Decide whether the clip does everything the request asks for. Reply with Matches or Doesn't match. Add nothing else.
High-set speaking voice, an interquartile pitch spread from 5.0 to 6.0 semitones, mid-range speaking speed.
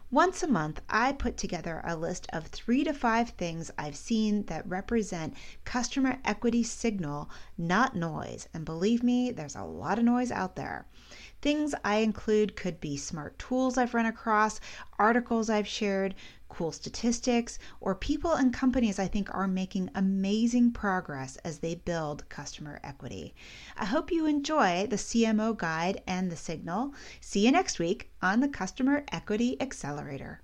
Matches